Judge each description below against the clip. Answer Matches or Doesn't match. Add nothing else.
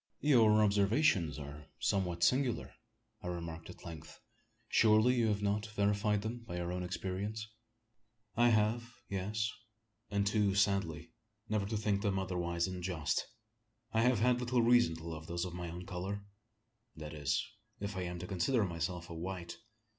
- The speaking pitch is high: Doesn't match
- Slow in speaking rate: Doesn't match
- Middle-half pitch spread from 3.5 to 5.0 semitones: Matches